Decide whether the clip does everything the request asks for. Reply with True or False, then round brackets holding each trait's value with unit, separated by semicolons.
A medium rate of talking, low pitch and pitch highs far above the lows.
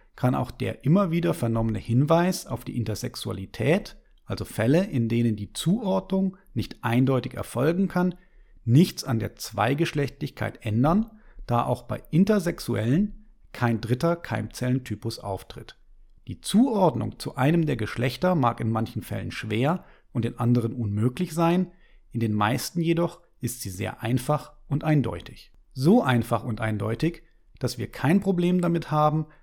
True (140 wpm; 130 Hz; 6.6 semitones)